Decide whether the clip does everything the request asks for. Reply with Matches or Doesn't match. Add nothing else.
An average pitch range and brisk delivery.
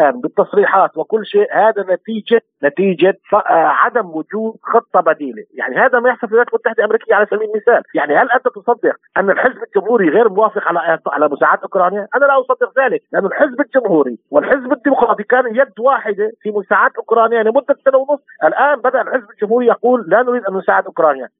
Matches